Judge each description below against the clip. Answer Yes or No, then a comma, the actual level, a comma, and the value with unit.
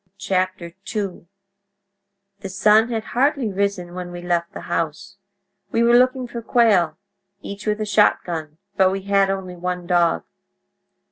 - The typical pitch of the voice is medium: No, high, 195 Hz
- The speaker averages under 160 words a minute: Yes, average, 140 wpm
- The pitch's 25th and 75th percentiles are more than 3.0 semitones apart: Yes, average, 3.4 semitones